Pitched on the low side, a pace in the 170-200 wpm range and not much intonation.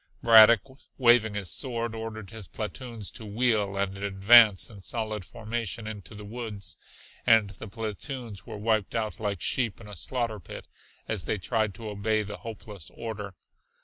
No: low, 110 Hz; average, 160 wpm; narrow, 2.2 semitones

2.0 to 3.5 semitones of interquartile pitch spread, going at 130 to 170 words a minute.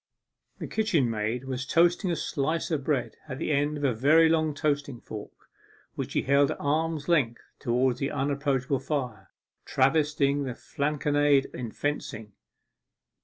Yes: average, 2.8 semitones; average, 150 wpm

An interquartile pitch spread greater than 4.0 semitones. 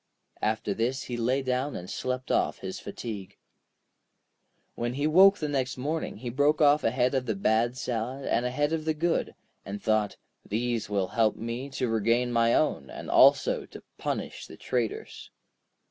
No: average, 3.5 semitones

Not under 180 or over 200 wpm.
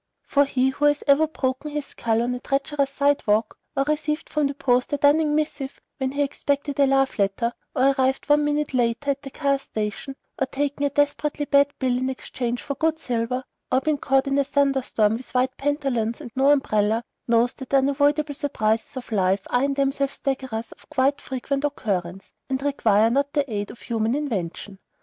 Yes: average, 195 wpm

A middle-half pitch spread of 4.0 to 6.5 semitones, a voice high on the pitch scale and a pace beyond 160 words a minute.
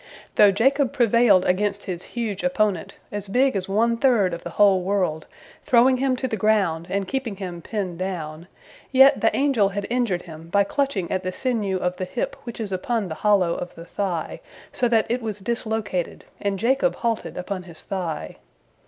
Yes: average, 4.4 semitones; high, 200 Hz; average, 190 wpm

